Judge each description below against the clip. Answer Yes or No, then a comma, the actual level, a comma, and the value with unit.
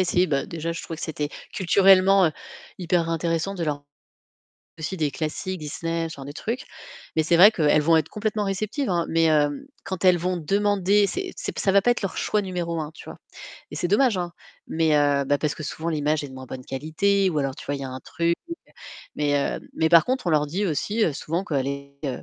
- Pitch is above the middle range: No, medium, 165 Hz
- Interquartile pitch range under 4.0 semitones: No, average, 4.3 semitones